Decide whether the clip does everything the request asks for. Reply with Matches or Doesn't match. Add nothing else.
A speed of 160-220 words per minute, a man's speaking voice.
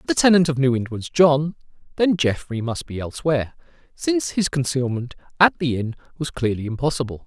Matches